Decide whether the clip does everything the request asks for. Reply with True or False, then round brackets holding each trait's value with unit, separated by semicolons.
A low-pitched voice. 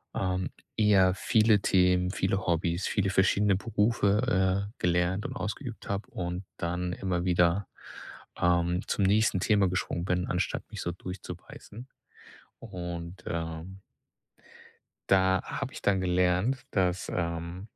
True (95 Hz)